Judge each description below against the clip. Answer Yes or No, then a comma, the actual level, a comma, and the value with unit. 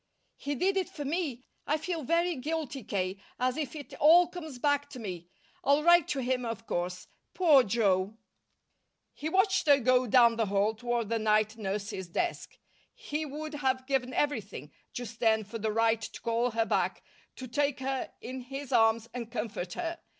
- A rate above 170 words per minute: Yes, average, 180 wpm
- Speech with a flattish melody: No, average, 4.9 semitones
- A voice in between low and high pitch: No, very high, 250 Hz